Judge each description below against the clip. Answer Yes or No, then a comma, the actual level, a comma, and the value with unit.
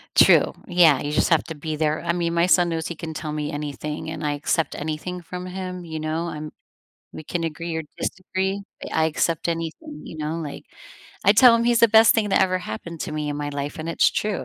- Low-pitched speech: No, medium, 165 Hz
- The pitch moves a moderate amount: Yes, average, 3.0 semitones